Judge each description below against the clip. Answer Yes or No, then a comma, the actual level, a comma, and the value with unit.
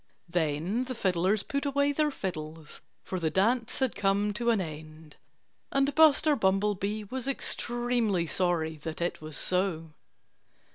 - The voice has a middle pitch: No, high, 195 Hz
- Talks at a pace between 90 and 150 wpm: Yes, average, 140 wpm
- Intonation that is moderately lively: No, wide, 6.8 semitones